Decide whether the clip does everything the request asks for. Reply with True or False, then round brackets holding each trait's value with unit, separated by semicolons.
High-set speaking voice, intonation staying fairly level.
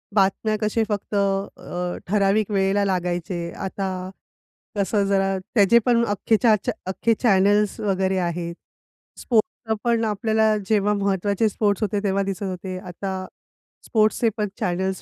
True (200 Hz; 2.1 semitones)